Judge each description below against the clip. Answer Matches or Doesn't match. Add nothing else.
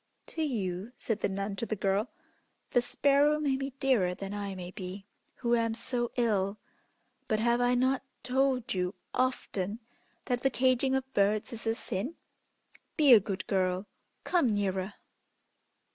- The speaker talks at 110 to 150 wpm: Doesn't match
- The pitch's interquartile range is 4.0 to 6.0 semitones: Matches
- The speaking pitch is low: Doesn't match